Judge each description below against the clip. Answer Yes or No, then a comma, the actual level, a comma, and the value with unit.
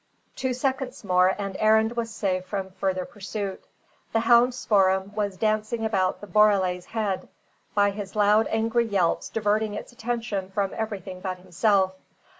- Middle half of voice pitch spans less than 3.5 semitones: Yes, average, 2.7 semitones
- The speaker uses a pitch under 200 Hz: No, high, 205 Hz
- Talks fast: No, average, 150 wpm